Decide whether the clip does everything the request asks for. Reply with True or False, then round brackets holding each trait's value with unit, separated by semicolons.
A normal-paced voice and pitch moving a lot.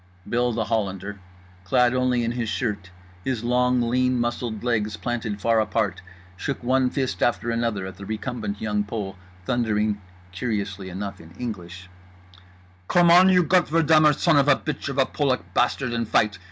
False (165 wpm; 3.6 semitones)